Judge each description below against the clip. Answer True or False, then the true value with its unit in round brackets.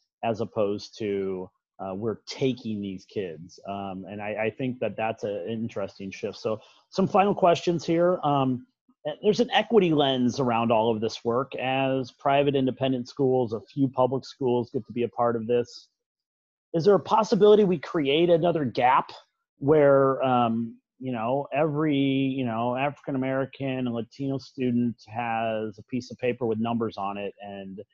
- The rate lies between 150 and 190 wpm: True (170 wpm)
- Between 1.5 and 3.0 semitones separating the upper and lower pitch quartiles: False (3.9 semitones)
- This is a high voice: False (130 Hz)